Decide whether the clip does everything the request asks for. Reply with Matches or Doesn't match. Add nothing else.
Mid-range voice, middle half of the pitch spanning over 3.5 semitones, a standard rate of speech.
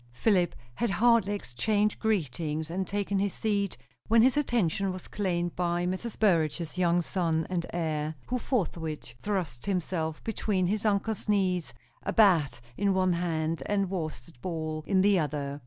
Matches